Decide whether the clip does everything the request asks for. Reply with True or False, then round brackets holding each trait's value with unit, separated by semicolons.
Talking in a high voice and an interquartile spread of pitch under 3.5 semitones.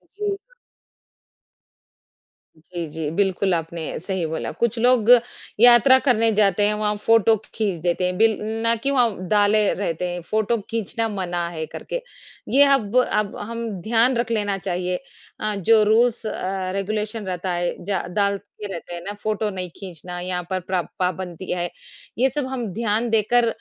False (205 Hz; 4.0 semitones)